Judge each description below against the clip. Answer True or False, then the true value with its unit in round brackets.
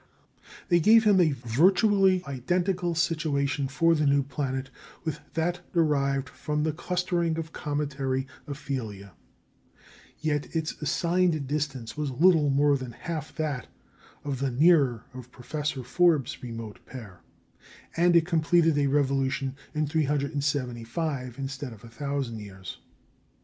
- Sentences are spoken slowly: True (125 wpm)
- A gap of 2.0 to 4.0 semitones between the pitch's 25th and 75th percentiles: True (3.7 semitones)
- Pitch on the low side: False (145 Hz)